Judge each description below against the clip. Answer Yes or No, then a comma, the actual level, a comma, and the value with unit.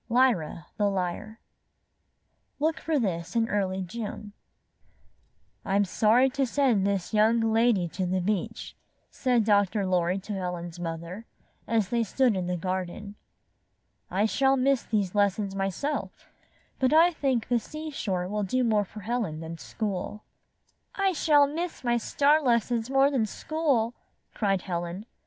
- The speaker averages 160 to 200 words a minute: No, average, 140 wpm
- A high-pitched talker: Yes, high, 215 Hz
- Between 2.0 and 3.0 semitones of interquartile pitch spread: No, average, 5.2 semitones